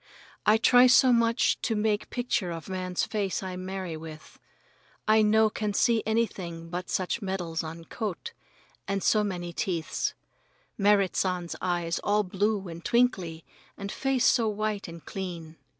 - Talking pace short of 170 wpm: Yes, average, 150 wpm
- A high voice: Yes, high, 195 Hz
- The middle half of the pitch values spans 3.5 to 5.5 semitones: Yes, average, 3.9 semitones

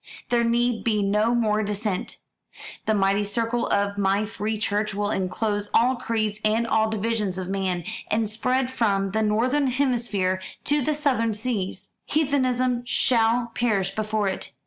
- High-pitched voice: Yes, high, 220 Hz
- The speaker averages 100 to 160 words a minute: Yes, average, 150 wpm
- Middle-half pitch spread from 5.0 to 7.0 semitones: No, average, 2.9 semitones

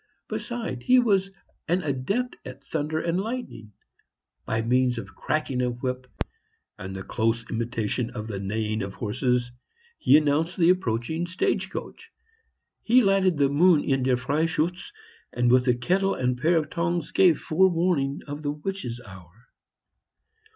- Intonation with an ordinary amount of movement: No, wide, 6.5 semitones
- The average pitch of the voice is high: No, medium, 140 Hz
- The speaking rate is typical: Yes, average, 150 wpm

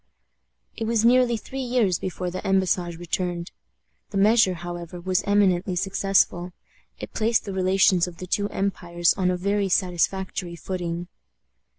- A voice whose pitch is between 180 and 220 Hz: Yes, medium, 185 Hz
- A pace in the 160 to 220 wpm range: No, average, 145 wpm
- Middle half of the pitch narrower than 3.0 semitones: Yes, narrow, 2.4 semitones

